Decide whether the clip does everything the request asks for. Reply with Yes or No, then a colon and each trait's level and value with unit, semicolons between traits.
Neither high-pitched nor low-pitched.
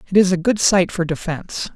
Yes: medium, 180 Hz